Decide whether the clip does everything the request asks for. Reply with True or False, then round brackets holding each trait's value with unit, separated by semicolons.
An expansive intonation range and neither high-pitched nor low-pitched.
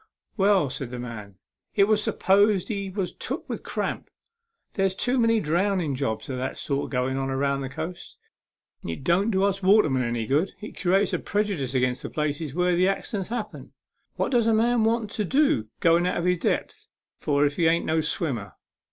True (6.7 semitones; 175 Hz)